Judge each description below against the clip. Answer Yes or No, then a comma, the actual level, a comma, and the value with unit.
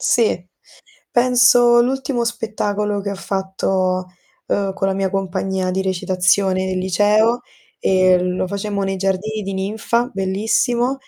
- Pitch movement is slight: No, average, 3.0 semitones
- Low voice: No, high, 195 Hz